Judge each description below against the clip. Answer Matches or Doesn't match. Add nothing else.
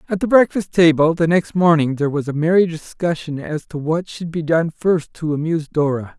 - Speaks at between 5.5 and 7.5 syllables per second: Doesn't match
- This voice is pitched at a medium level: Matches